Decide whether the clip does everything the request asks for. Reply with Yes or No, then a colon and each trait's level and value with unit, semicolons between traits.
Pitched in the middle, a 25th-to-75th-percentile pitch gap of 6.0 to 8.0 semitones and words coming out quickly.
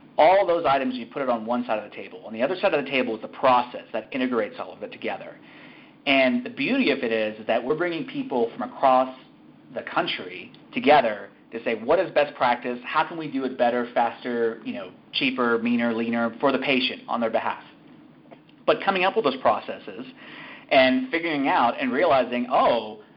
No: low, 130 Hz; wide, 7.7 semitones; fast, 210 wpm